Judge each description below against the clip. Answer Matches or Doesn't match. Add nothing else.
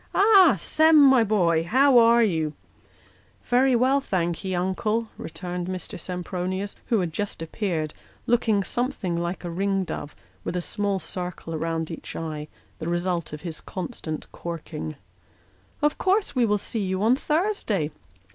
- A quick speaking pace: Doesn't match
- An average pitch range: Doesn't match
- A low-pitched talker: Doesn't match